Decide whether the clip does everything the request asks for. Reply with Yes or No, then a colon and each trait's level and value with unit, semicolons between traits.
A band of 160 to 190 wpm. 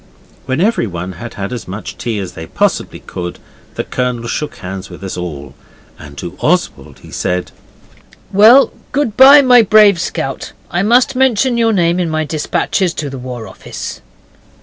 Yes: average, 170 wpm